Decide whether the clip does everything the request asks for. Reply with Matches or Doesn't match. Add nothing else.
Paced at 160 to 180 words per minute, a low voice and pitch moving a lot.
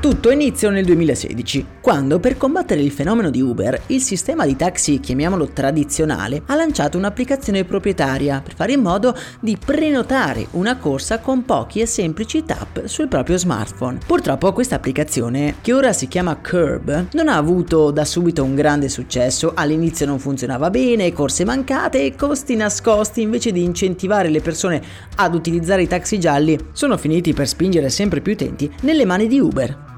Doesn't match